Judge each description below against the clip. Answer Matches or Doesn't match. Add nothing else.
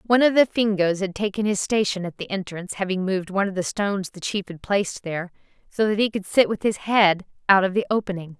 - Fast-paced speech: Matches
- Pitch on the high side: Matches